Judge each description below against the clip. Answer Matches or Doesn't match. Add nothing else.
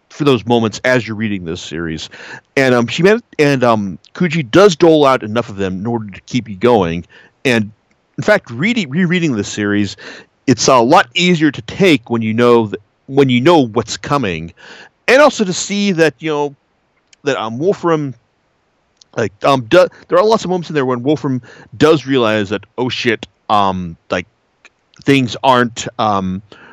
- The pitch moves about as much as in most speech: Doesn't match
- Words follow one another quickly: Doesn't match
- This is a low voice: Matches